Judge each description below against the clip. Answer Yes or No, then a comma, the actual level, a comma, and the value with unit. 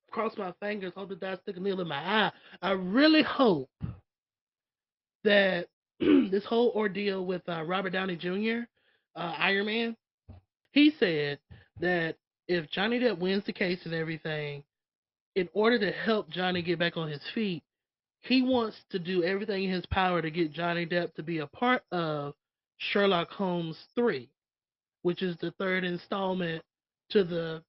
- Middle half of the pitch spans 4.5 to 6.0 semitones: No, average, 3.8 semitones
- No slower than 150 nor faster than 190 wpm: Yes, average, 165 wpm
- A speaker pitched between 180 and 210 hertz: Yes, medium, 185 Hz